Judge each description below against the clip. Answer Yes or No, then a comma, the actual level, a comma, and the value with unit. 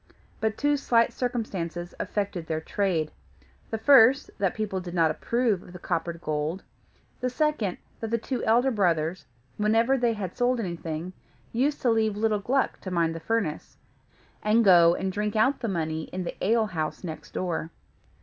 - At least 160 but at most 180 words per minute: Yes, average, 170 wpm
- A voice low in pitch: No, high, 205 Hz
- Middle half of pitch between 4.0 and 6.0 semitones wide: Yes, average, 5.1 semitones